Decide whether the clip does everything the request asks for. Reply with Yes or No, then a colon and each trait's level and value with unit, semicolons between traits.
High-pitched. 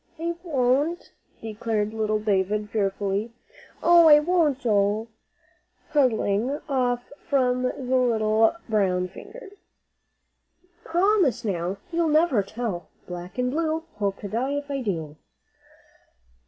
Yes: high, 240 Hz